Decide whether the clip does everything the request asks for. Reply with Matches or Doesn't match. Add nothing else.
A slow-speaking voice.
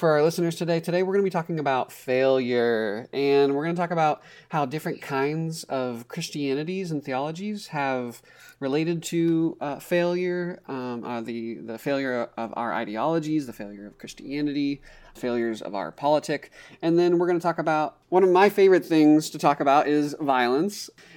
Doesn't match